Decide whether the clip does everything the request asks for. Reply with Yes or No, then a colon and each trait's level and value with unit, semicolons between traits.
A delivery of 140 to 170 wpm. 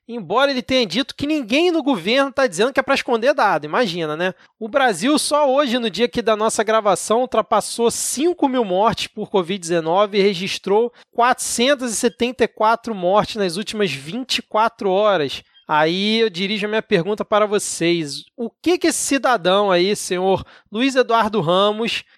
Yes: average, 160 wpm